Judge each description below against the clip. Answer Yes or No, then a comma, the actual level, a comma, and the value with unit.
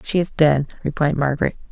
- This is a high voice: No, medium, 150 Hz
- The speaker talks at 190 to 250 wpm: No, average, 175 wpm